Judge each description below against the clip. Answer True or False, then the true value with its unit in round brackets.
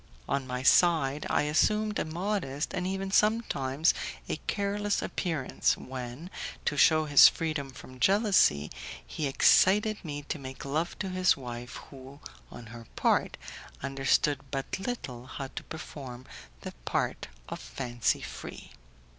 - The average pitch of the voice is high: False (145 Hz)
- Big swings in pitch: True (6.0 semitones)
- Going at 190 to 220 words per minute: False (140 wpm)